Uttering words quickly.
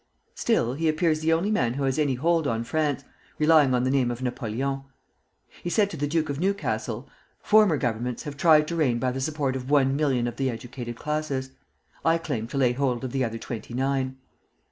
Yes: fast, 210 wpm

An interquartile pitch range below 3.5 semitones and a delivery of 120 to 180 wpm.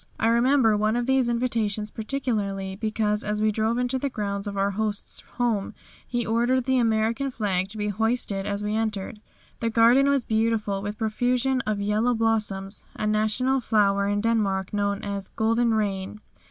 Yes: narrow, 2.6 semitones; average, 175 wpm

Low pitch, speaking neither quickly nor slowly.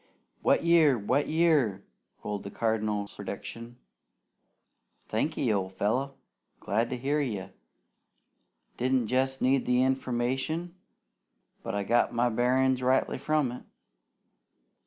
No: low, 125 Hz; slow, 115 wpm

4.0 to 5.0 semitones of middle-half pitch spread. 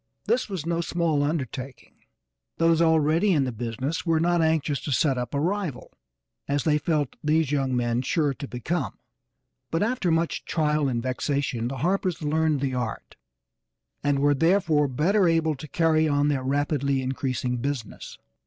No: average, 3.5 semitones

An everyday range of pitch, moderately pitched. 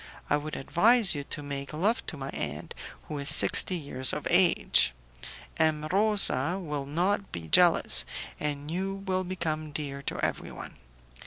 Yes: average, 4.7 semitones; medium, 155 Hz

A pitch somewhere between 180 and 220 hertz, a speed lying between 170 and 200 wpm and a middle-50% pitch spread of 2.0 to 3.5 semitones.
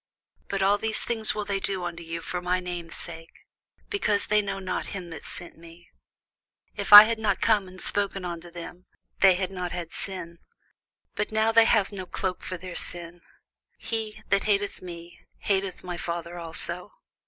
Yes: medium, 185 Hz; average, 180 wpm; average, 2.9 semitones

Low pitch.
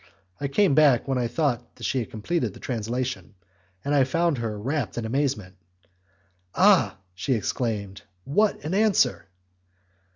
Yes: low, 130 Hz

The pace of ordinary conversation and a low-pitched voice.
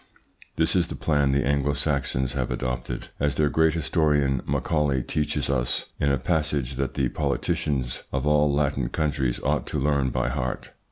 Yes: average, 170 wpm; very low, 70 Hz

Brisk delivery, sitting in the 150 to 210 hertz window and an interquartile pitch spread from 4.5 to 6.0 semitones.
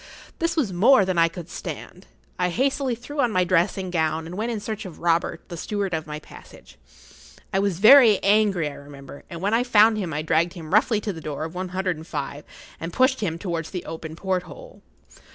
Yes: fast, 215 wpm; medium, 185 Hz; average, 4.8 semitones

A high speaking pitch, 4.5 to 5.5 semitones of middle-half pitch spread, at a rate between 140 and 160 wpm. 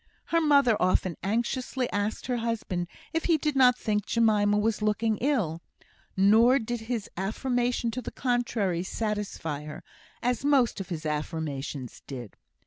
Yes: high, 220 Hz; average, 5.0 semitones; average, 145 wpm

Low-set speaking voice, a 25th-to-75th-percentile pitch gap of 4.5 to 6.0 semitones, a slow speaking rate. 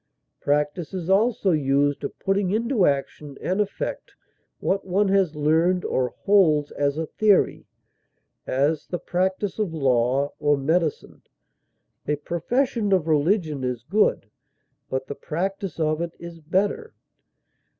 No: medium, 170 Hz; average, 5.0 semitones; slow, 130 wpm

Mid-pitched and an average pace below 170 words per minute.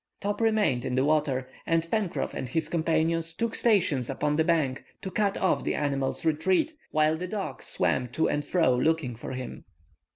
No: medium, 160 Hz; average, 185 wpm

